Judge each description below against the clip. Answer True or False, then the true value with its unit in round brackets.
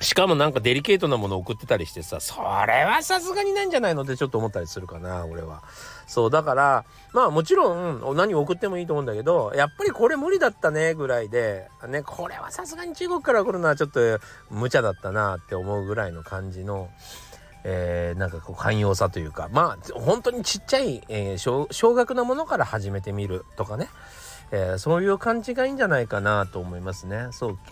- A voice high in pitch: False (130 Hz)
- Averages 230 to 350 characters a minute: False (435 characters per minute)